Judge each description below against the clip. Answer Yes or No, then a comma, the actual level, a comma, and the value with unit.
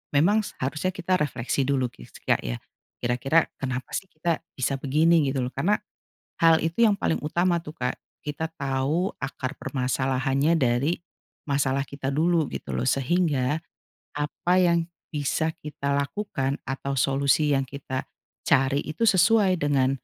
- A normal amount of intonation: Yes, average, 3.8 semitones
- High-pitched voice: No, medium, 145 Hz